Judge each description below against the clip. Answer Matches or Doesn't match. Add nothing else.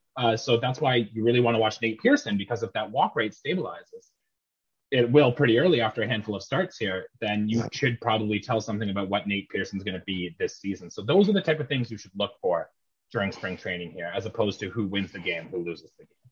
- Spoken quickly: Matches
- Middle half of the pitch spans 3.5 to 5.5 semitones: Matches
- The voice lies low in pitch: Matches